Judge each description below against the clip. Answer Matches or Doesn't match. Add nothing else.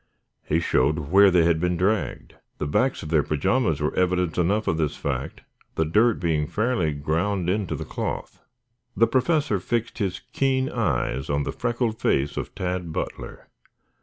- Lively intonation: Matches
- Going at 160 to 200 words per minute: Matches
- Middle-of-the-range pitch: Doesn't match